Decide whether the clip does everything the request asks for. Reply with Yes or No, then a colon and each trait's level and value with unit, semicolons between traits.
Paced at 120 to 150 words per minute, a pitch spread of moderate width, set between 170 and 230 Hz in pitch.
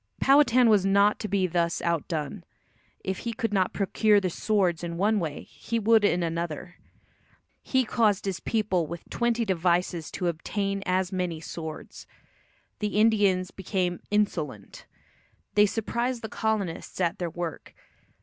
Yes: average, 145 wpm; average, 3.8 semitones; high, 190 Hz